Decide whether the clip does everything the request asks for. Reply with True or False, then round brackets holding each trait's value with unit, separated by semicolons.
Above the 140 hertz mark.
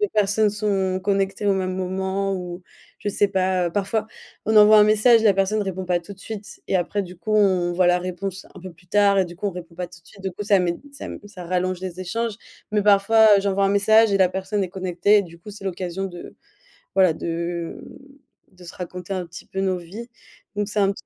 True (190 Hz)